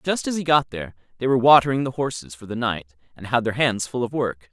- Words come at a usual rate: No, fast, 265 wpm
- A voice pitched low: Yes, low, 125 Hz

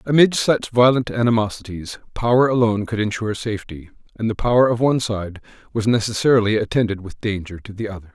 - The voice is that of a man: Yes, male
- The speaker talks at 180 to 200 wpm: No, average, 170 wpm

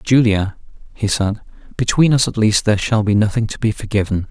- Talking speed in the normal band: Yes, average, 195 wpm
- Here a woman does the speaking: No, male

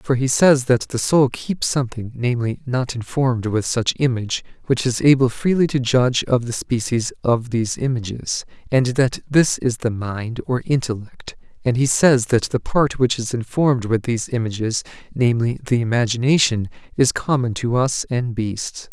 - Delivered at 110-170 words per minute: Yes, average, 160 wpm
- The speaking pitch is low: Yes, low, 125 Hz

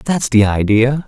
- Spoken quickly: No, average, 170 wpm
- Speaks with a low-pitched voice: Yes, low, 120 Hz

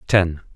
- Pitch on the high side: No, very low, 85 Hz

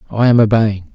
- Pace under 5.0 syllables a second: No, 5.5 syllables/s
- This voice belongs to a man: Yes, male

